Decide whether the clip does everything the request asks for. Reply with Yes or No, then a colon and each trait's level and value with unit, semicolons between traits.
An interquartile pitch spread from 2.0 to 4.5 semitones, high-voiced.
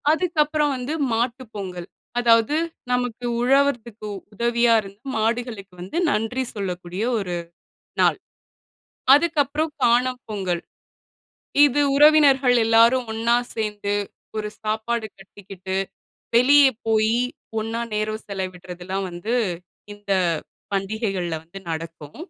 Yes: average, 4.1 semitones; high, 225 Hz